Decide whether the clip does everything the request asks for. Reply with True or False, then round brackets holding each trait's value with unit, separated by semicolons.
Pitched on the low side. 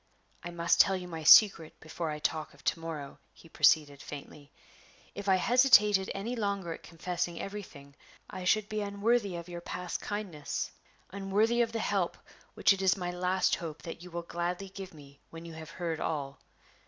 False (180 Hz)